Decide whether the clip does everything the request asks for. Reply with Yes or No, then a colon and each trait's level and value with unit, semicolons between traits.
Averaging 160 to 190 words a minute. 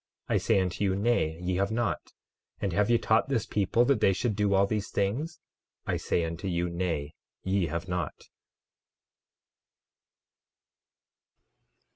No: average, 145 wpm